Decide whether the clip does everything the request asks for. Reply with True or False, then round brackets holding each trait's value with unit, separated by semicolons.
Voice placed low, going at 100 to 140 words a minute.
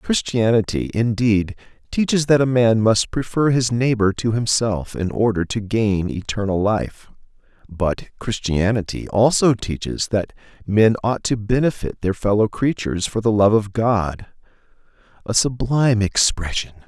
True (110 Hz; 135 wpm)